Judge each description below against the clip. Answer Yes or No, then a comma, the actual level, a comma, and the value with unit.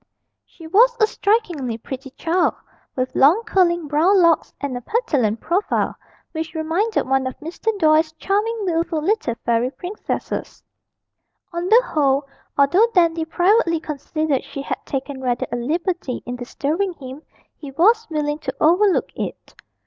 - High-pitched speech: Yes, very high, 320 Hz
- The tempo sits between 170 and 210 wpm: No, average, 145 wpm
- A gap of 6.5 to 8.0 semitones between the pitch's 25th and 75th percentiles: No, average, 5.2 semitones